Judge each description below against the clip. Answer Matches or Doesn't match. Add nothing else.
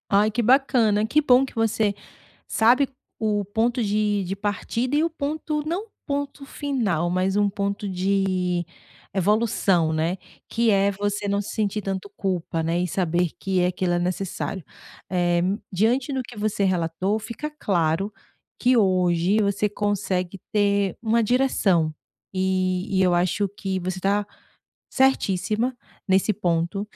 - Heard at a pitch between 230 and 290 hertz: Doesn't match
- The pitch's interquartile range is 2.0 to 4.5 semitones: Matches